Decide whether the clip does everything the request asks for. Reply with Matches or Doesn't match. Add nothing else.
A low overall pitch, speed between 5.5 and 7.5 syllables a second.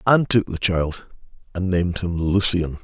Doesn't match